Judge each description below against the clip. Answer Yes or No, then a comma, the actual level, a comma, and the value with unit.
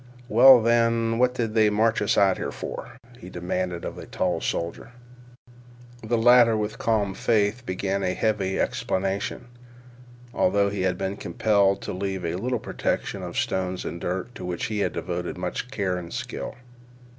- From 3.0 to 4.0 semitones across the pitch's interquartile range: Yes, average, 3.7 semitones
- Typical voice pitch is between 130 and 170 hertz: No, low, 100 Hz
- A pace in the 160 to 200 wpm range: Yes, average, 170 wpm